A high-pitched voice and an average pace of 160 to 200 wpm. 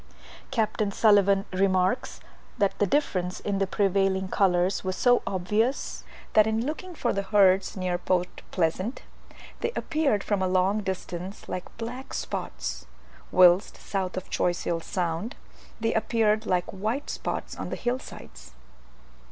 No: high, 195 Hz; average, 140 wpm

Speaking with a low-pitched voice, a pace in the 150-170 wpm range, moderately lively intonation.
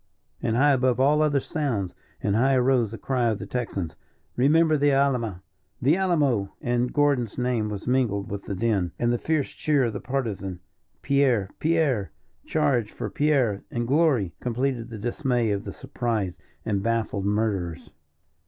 Yes: low, 120 Hz; average, 160 wpm; average, 4.8 semitones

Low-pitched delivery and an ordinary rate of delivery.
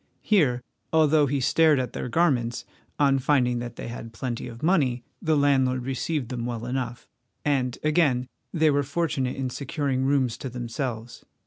Yes: low, 130 Hz; average, 160 wpm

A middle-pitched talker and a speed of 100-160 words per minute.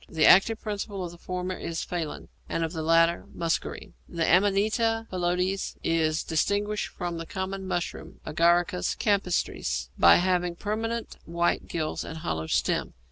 Yes: medium, 180 Hz; average, 150 wpm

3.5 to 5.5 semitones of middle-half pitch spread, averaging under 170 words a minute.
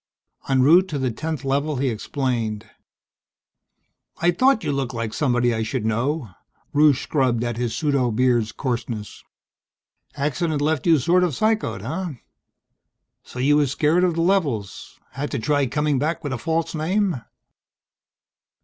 Yes: average, 4.6 semitones; average, 150 wpm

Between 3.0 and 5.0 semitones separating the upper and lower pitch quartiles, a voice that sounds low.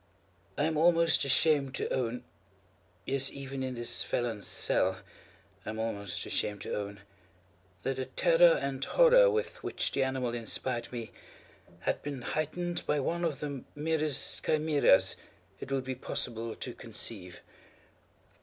No: wide, 5.6 semitones; low, 130 Hz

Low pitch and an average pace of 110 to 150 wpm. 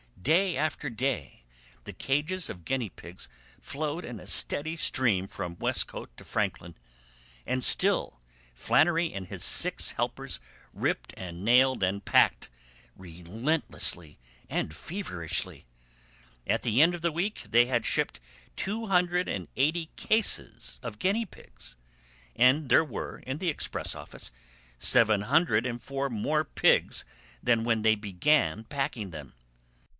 Yes: low, 125 Hz; slow, 135 wpm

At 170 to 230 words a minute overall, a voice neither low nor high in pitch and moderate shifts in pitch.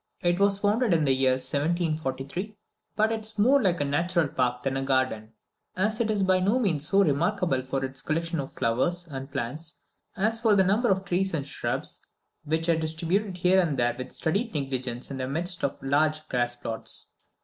No: average, 195 wpm; medium, 165 Hz; wide, 6.2 semitones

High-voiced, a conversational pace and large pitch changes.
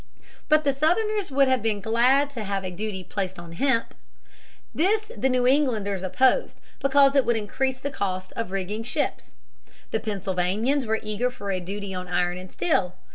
Yes: high, 220 Hz; average, 180 wpm; wide, 6.1 semitones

